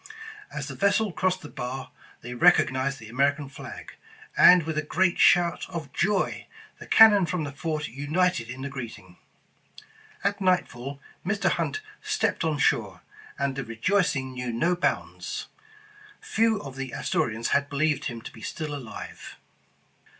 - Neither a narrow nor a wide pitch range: No, wide, 5.8 semitones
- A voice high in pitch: No, medium, 145 Hz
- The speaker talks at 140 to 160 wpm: Yes, average, 155 wpm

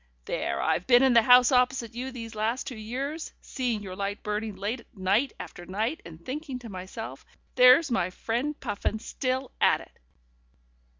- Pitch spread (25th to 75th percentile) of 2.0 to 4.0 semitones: Yes, average, 3.7 semitones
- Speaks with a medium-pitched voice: No, high, 235 Hz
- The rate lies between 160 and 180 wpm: Yes, average, 170 wpm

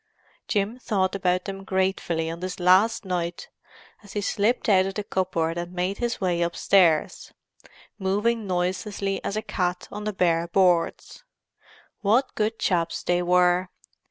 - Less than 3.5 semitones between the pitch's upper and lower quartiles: Yes, narrow, 2.5 semitones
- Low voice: No, medium, 185 Hz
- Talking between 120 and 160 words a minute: Yes, average, 150 wpm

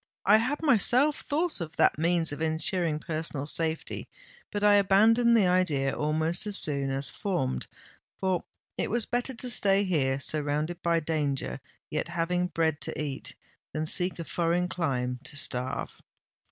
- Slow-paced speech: No, average, 155 wpm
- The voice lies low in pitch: No, medium, 165 Hz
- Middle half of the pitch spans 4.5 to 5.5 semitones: Yes, average, 4.8 semitones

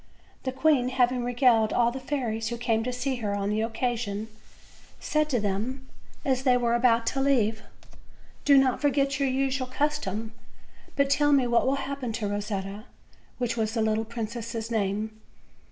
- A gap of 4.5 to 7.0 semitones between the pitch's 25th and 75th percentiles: No, average, 3.2 semitones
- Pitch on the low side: No, high, 240 Hz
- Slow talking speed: No, average, 170 wpm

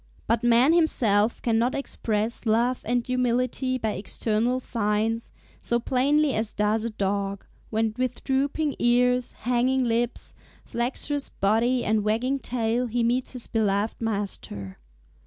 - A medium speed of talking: No, slow, 130 wpm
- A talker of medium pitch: No, high, 235 Hz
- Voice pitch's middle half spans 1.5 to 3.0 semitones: Yes, narrow, 2.6 semitones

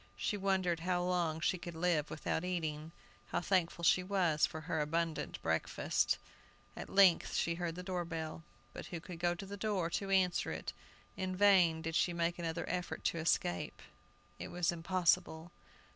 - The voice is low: No, medium, 175 Hz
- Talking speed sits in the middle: Yes, average, 175 wpm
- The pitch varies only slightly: Yes, narrow, 2.0 semitones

